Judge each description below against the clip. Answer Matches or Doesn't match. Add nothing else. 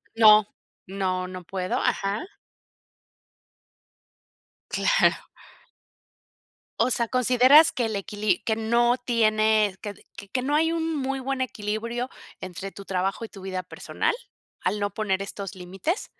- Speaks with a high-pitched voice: Matches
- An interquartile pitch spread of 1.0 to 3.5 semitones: Doesn't match